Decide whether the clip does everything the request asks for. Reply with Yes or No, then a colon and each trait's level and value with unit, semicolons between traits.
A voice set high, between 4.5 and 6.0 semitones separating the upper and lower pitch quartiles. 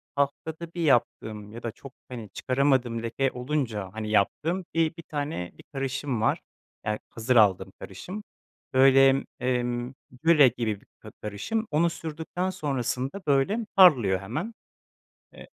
No: low, 130 Hz; wide, 5.6 semitones